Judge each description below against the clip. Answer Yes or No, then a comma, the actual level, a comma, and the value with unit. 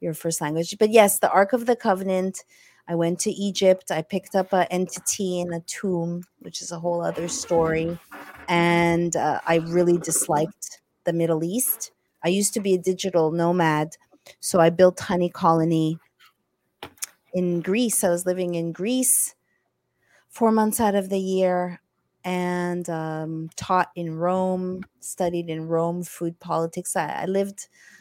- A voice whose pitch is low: No, medium, 175 Hz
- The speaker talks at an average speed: Yes, average, 160 wpm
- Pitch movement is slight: Yes, narrow, 2.2 semitones